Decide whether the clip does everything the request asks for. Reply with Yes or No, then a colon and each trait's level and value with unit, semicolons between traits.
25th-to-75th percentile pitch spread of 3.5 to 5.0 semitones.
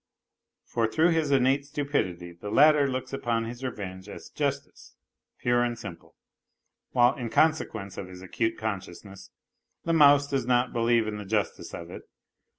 No: wide, 5.5 semitones